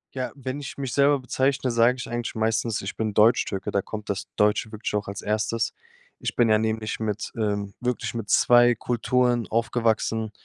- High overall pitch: No, low, 115 Hz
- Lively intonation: No, narrow, 2.4 semitones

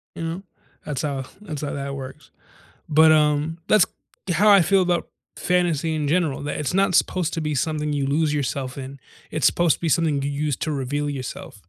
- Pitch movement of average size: Yes, average, 3.0 semitones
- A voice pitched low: No, medium, 150 Hz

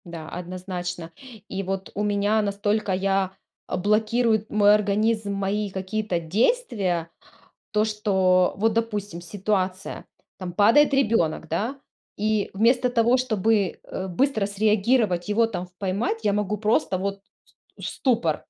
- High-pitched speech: Yes, high, 205 Hz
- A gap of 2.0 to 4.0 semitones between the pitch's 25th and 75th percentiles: Yes, average, 2.8 semitones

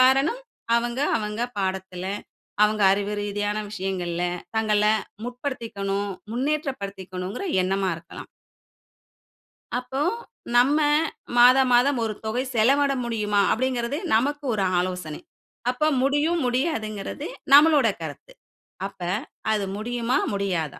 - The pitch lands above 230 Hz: No, high, 220 Hz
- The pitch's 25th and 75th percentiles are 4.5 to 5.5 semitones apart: Yes, average, 4.9 semitones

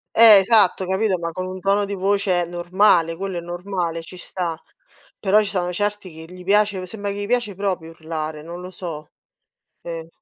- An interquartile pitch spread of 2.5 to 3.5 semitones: Yes, average, 2.9 semitones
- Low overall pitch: No, medium, 185 Hz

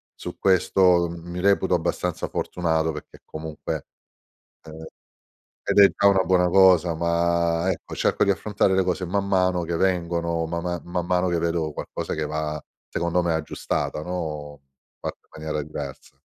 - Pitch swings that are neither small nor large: No, narrow, 2.2 semitones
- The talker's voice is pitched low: Yes, very low, 85 Hz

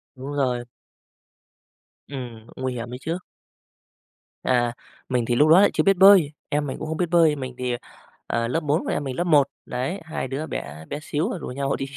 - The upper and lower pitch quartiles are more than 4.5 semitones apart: No, average, 4.2 semitones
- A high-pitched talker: No, medium, 140 Hz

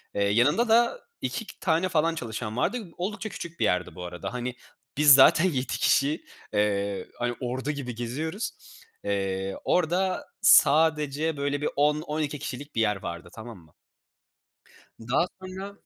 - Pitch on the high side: No, medium, 145 Hz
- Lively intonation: Yes, wide, 6.5 semitones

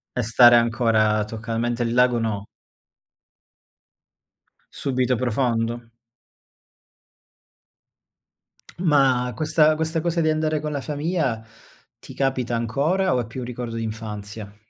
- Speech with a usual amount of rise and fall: Yes, average, 4.5 semitones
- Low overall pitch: Yes, low, 120 Hz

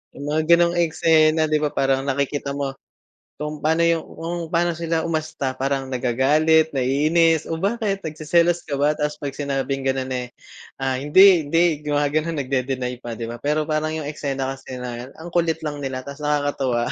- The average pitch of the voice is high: No, medium, 150 Hz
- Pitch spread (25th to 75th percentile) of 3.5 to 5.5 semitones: No, average, 3.1 semitones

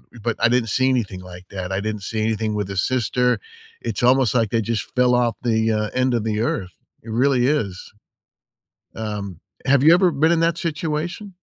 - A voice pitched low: Yes, low, 115 Hz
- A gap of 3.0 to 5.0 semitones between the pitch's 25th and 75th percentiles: Yes, average, 3.8 semitones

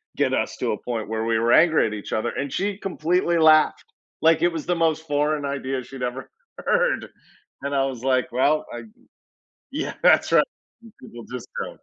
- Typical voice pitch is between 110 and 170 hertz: Yes, medium, 140 Hz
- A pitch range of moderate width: Yes, average, 4.8 semitones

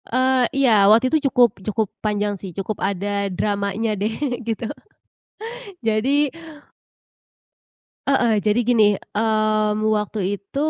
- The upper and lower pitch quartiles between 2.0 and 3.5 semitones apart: Yes, average, 3.0 semitones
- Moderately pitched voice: No, high, 215 Hz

